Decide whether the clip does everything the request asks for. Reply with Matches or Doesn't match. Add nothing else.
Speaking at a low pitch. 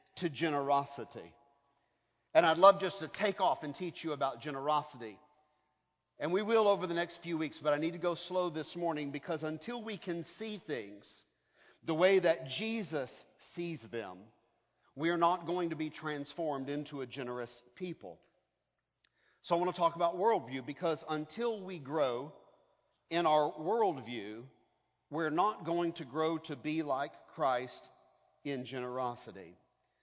Doesn't match